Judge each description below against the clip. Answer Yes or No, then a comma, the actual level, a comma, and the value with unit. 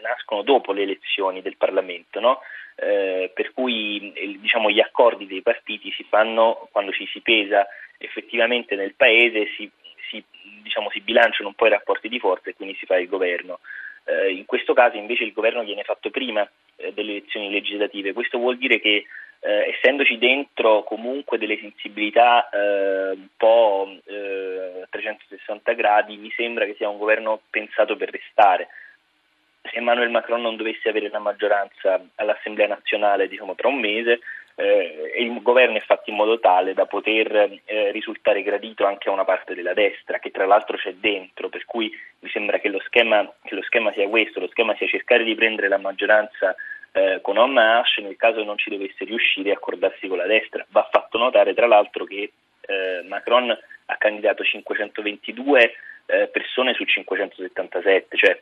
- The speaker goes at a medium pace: No, fast, 175 wpm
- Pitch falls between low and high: No, low, 110 Hz